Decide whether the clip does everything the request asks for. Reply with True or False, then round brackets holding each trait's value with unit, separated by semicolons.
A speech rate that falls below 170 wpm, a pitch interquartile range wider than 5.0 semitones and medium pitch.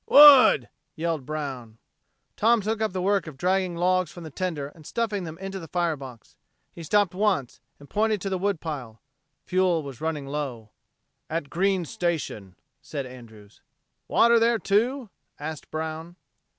True (160 wpm; 5.6 semitones; 170 Hz)